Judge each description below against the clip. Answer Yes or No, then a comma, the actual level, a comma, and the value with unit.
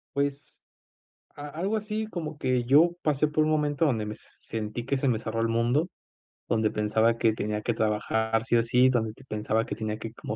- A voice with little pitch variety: No, average, 4.8 semitones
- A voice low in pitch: Yes, low, 120 Hz